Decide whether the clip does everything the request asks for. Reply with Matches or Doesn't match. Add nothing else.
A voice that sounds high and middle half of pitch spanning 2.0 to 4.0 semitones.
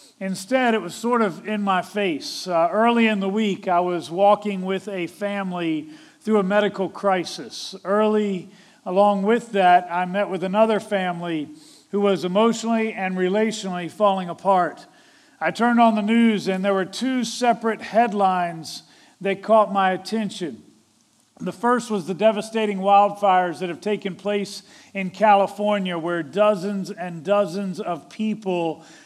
Matches